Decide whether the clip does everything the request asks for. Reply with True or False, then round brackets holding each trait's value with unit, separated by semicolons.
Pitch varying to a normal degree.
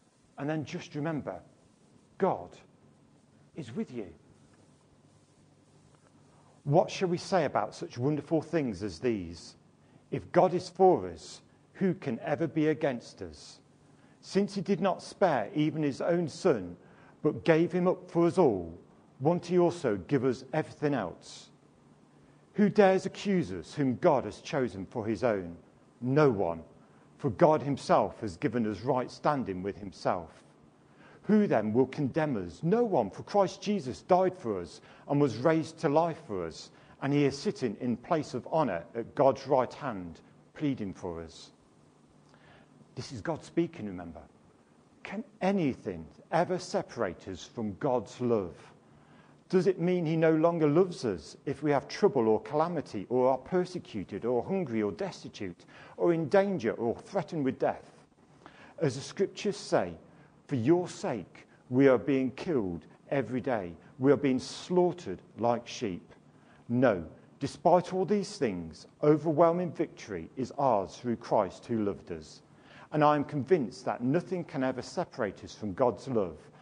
False (6.5 semitones)